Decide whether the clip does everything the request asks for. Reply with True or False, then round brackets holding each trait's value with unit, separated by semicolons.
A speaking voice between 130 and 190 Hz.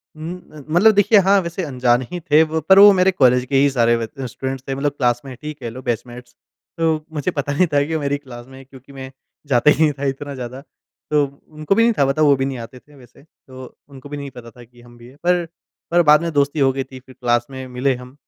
True (135 Hz)